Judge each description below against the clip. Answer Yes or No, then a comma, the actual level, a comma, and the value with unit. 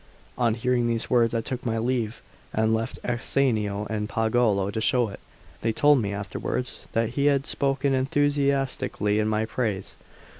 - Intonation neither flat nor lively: Yes, average, 3.1 semitones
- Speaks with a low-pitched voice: Yes, low, 115 Hz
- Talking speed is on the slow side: No, average, 160 wpm